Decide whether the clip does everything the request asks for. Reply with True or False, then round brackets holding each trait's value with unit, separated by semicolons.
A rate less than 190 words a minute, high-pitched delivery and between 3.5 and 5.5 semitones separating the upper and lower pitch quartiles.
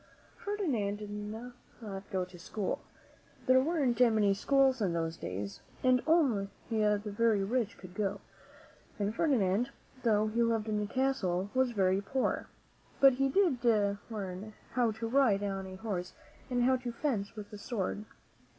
True (155 wpm; 215 Hz; 4.3 semitones)